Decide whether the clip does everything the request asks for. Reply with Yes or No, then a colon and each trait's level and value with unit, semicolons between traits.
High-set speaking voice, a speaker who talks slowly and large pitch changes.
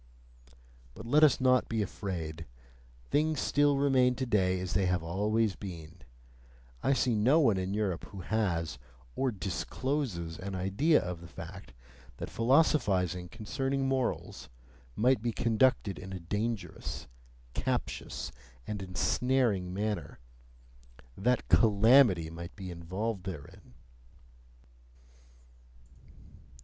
No: low, 105 Hz; slow, 115 wpm; wide, 5.8 semitones